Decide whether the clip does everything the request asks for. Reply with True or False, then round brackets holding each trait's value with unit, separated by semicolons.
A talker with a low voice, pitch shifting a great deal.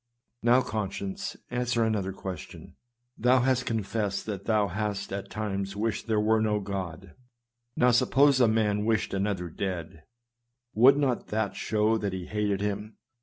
False (105 Hz; 2.7 semitones)